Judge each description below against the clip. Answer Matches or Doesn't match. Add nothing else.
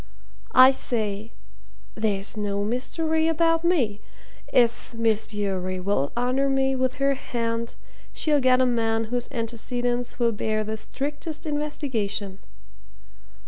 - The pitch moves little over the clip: Doesn't match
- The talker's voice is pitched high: Matches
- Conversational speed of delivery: Doesn't match